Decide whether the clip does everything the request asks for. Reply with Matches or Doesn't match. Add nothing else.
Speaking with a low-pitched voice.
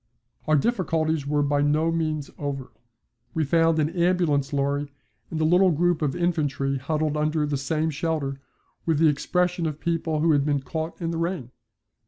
Doesn't match